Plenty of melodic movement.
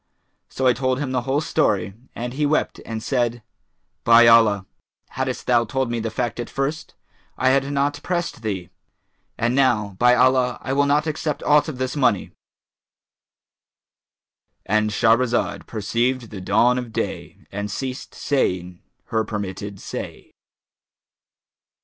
No: average, 3.4 semitones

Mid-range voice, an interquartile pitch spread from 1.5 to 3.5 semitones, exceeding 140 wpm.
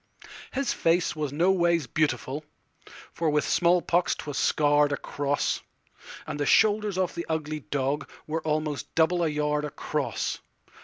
No: medium, 155 Hz; narrow, 2.6 semitones; slow, 135 wpm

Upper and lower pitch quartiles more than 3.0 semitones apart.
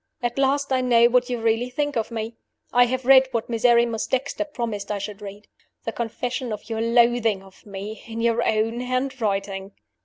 No: narrow, 2.5 semitones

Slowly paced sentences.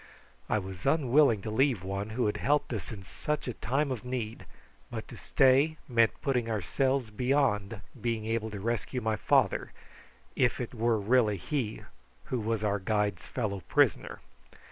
No: average, 165 wpm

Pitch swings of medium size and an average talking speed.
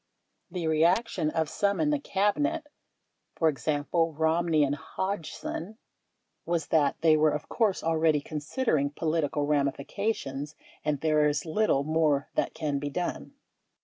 No: average, 3.3 semitones; slow, 130 wpm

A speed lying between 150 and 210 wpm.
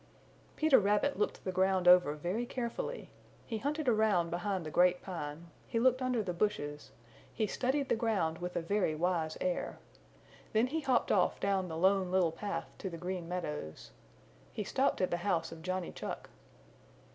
Yes: average, 175 wpm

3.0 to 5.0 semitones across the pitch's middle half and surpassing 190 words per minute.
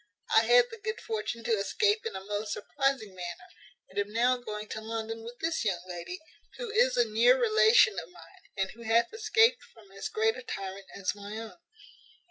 Yes: average, 4.0 semitones; average, 200 wpm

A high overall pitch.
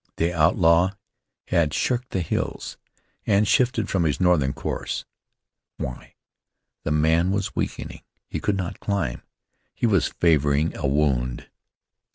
No: very low, 85 Hz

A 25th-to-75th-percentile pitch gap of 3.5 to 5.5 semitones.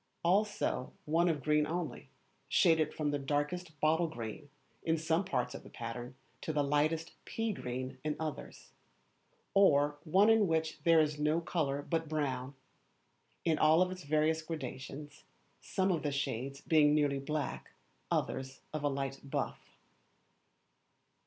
No: narrow, 2.6 semitones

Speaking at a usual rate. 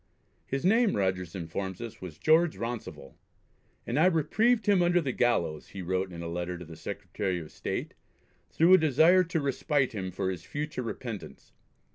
Yes: average, 175 wpm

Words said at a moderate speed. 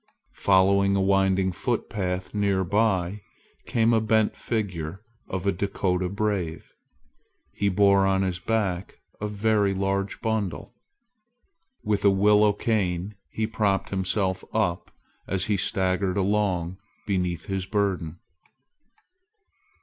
No: slow, 115 wpm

